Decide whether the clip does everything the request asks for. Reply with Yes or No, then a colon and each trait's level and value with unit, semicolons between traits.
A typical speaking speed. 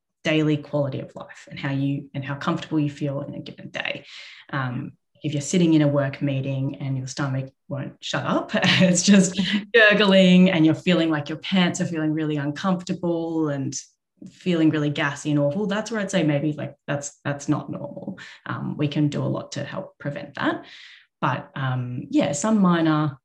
Yes: average, 190 wpm